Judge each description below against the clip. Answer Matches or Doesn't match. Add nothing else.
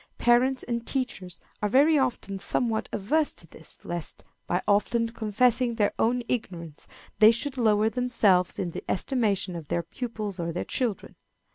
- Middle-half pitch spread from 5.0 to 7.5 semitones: Doesn't match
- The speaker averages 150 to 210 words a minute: Matches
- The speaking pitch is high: Matches